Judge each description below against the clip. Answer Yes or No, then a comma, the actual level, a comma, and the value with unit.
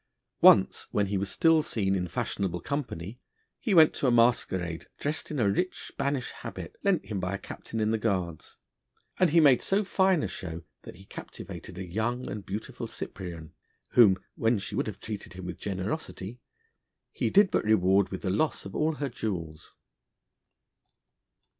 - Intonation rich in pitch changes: Yes, wide, 6.9 semitones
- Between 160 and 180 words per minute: Yes, average, 175 wpm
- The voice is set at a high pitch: No, low, 105 Hz